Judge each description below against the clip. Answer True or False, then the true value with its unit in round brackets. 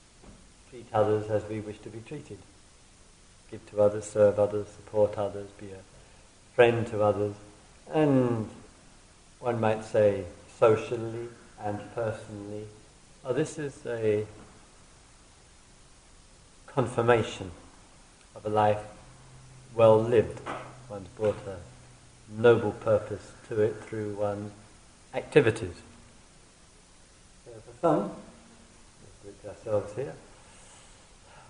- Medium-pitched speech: False (105 Hz)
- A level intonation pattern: True (2.3 semitones)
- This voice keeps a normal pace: False (105 wpm)